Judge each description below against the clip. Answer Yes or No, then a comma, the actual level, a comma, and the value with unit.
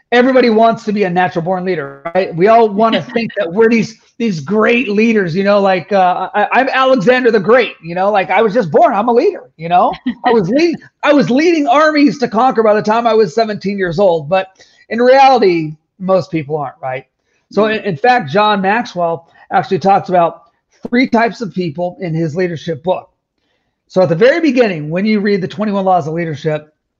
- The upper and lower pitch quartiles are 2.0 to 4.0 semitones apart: No, average, 4.4 semitones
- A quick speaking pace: Yes, fast, 210 wpm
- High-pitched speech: Yes, high, 205 Hz